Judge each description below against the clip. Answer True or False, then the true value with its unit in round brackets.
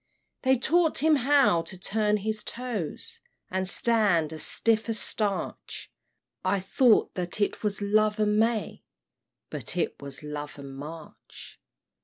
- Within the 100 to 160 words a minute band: True (140 wpm)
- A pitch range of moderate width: True (4.9 semitones)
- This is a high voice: True (210 Hz)